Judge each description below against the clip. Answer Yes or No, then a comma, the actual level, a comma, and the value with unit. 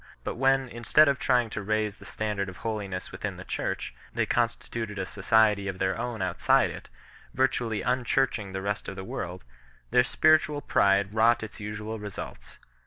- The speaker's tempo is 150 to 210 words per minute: Yes, average, 175 wpm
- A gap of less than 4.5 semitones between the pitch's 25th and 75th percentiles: Yes, average, 3.5 semitones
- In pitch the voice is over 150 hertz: No, low, 110 Hz